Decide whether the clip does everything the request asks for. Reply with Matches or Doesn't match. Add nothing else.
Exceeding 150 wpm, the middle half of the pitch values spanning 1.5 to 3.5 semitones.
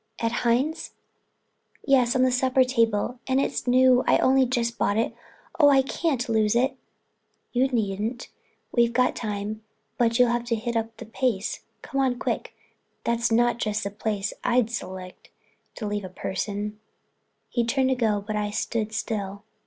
Matches